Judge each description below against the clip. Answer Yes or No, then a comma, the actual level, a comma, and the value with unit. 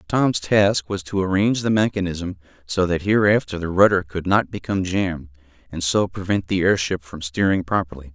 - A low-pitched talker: Yes, very low, 90 Hz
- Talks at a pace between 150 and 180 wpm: Yes, average, 175 wpm